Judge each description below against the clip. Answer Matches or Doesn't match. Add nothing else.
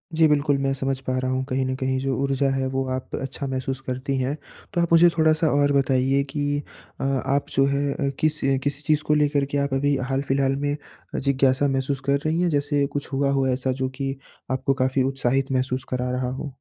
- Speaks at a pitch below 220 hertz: Matches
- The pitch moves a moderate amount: Doesn't match